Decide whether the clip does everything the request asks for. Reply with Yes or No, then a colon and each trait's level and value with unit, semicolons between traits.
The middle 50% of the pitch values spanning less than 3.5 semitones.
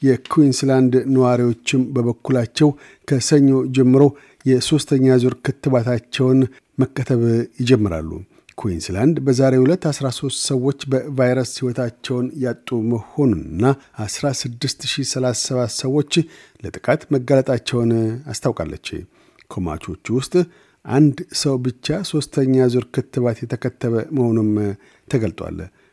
Yes: narrow, 2.4 semitones